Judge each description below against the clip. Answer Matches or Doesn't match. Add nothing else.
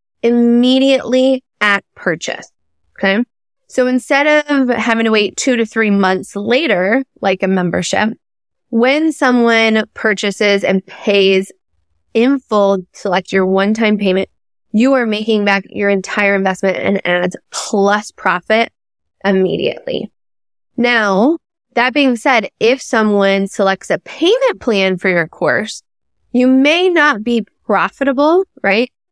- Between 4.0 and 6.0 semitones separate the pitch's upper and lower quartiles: Matches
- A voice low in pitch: Doesn't match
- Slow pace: Matches